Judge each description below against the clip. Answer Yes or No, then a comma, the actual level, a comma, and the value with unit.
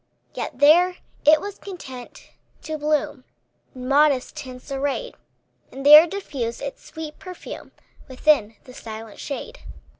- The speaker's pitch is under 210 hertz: No, very high, 290 Hz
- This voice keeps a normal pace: No, slow, 125 wpm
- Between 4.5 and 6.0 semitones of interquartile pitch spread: No, average, 3.6 semitones